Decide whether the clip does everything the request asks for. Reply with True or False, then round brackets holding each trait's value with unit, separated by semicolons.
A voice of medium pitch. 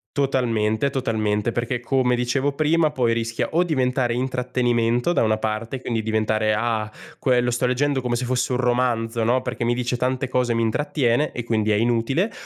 False (120 Hz)